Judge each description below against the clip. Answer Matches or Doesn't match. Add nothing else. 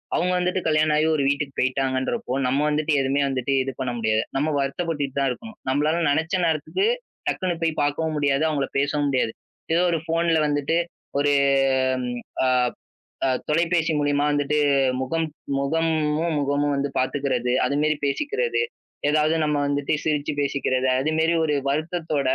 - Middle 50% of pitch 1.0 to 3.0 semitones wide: Matches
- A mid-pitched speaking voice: Matches